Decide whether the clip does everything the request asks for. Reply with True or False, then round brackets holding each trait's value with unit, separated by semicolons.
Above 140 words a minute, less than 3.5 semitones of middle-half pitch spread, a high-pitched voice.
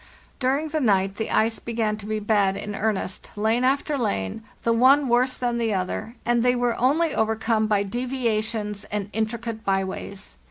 True (175 wpm; 2.8 semitones; 225 Hz)